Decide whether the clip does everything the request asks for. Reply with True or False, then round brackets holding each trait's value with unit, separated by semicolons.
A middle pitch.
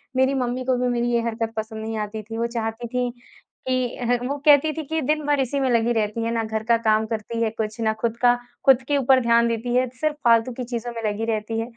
False (235 Hz)